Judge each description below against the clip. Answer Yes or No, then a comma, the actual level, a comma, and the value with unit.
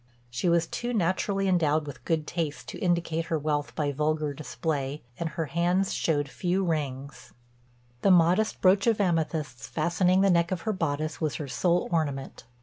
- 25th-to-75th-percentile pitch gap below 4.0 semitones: Yes, average, 3.3 semitones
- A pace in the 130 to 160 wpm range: No, average, 170 wpm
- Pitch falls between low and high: Yes, medium, 165 Hz